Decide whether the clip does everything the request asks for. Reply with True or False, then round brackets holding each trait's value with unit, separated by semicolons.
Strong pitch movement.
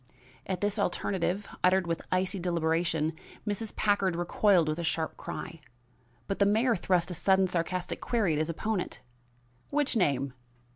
False (3.3 semitones)